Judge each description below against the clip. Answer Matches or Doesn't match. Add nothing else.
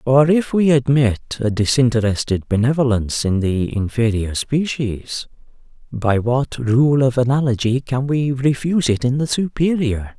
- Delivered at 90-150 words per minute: Matches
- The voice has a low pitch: Matches